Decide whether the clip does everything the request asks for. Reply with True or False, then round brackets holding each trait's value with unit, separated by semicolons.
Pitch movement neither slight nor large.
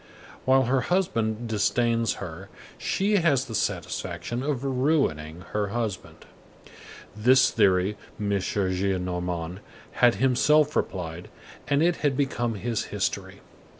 False (5.9 semitones)